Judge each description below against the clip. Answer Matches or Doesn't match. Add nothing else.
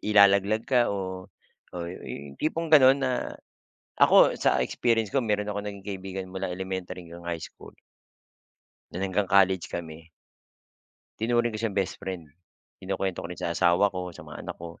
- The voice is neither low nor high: Doesn't match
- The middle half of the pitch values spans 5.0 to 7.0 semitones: Doesn't match